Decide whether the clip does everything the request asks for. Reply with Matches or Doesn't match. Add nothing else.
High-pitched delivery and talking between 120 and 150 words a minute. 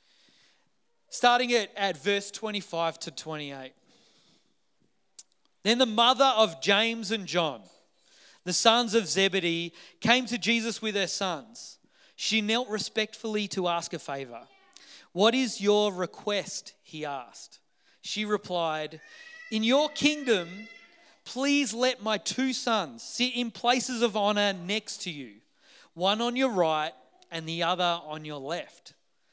Matches